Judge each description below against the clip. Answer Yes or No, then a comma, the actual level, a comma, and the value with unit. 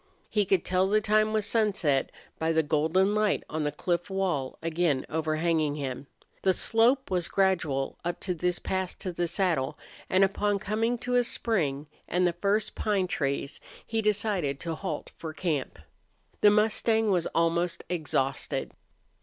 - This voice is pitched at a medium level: Yes, medium, 180 Hz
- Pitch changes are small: No, average, 4.7 semitones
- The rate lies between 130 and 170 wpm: Yes, average, 160 wpm